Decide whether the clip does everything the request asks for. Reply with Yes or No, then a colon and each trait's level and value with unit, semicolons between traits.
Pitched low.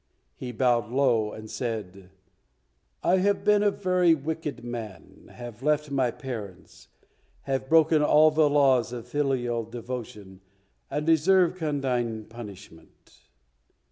Yes: low, 130 Hz